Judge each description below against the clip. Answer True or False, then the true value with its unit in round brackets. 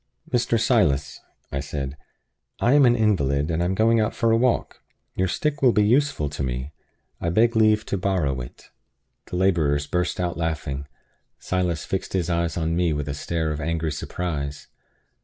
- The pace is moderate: True (180 wpm)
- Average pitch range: False (6.7 semitones)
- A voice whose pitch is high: False (85 Hz)